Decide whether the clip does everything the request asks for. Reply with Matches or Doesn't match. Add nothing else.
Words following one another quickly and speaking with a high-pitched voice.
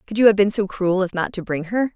Matches